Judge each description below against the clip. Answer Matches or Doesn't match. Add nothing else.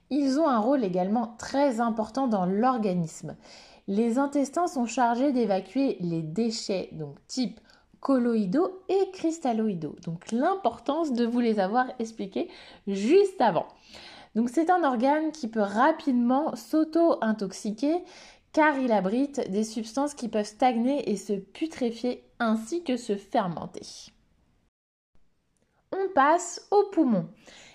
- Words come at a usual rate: Doesn't match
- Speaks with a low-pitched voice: Doesn't match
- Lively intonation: Doesn't match